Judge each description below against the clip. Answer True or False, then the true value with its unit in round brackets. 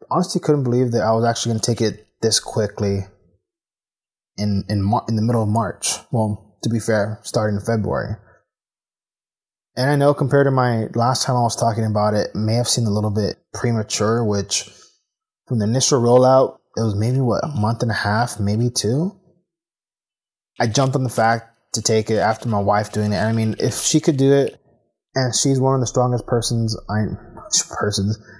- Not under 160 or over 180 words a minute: False (200 wpm)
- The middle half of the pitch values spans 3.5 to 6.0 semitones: False (3.1 semitones)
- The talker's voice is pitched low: True (115 Hz)